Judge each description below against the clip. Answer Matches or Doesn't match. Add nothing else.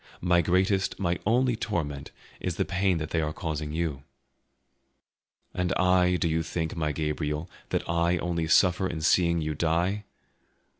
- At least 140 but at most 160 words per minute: Matches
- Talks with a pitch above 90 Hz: Doesn't match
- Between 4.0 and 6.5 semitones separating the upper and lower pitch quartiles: Doesn't match